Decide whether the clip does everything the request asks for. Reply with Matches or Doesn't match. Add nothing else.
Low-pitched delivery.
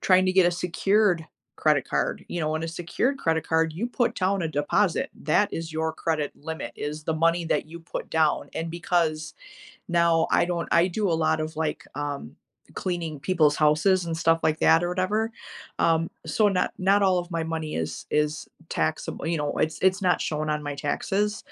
Doesn't match